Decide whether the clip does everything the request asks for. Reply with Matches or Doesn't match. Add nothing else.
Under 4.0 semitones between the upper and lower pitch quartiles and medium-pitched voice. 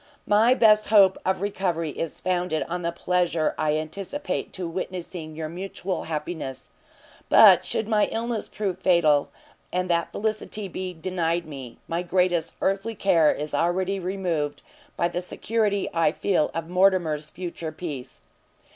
Matches